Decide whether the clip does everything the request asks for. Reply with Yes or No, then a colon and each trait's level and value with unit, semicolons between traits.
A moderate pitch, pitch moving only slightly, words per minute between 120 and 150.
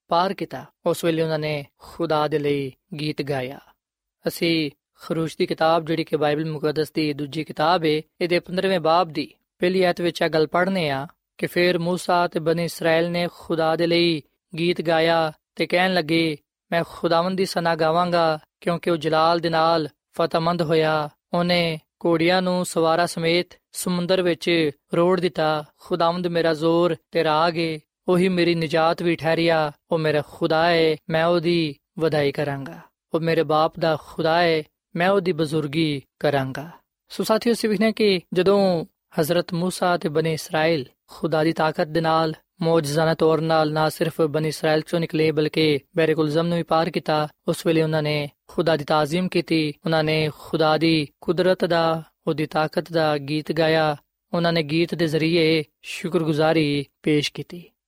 No: medium, 165 Hz; narrow, 1.9 semitones; average, 160 wpm